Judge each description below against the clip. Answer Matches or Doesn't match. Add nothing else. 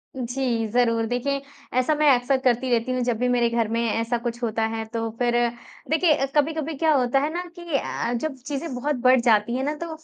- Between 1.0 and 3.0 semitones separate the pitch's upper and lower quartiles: Doesn't match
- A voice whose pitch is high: Matches